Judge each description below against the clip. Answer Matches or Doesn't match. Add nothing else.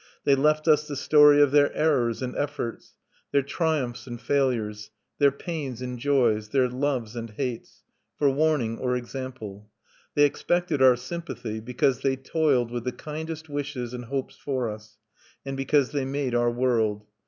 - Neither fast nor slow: Matches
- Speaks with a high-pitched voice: Doesn't match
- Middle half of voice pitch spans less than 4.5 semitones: Matches